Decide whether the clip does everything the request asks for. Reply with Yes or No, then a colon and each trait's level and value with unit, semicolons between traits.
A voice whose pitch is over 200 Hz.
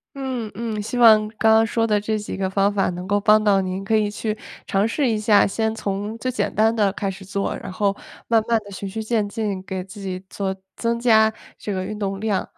Yes: high, 210 Hz